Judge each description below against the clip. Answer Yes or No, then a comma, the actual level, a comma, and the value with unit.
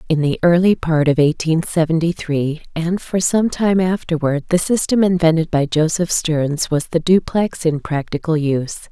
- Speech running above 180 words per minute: No, average, 170 wpm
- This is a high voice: No, medium, 165 Hz